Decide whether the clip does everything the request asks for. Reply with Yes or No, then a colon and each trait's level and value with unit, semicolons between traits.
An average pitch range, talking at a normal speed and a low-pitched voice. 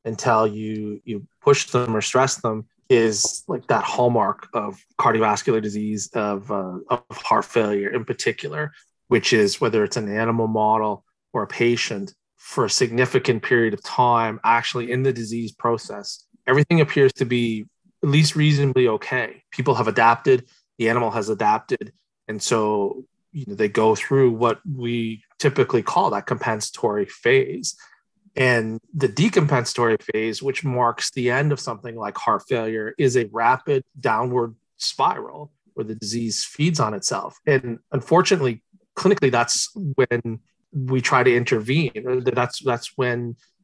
Yes: average, 4.0 semitones; average, 150 wpm; low, 120 Hz